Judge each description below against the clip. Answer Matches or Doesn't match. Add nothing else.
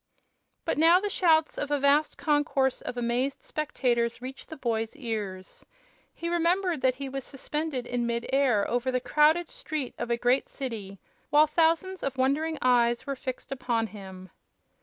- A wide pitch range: Doesn't match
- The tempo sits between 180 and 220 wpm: Doesn't match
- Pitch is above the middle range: Matches